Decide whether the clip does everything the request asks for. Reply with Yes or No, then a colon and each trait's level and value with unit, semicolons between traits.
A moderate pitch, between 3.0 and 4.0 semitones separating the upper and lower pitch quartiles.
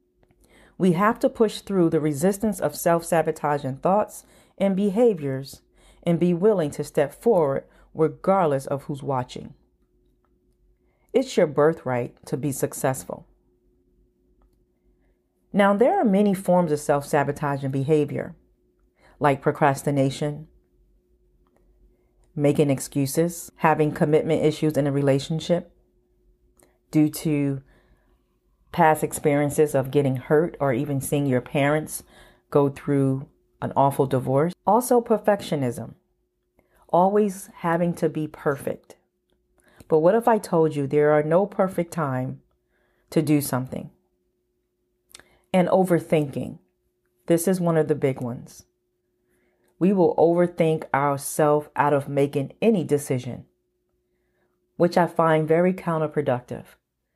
No: medium, 150 Hz; average, 4.9 semitones